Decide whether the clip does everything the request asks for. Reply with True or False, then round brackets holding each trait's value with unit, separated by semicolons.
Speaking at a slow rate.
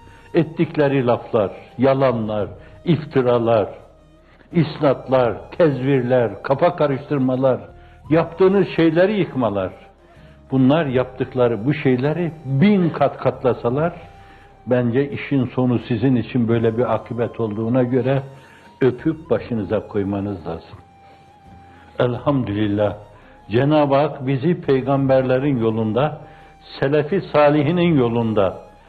True (85 wpm)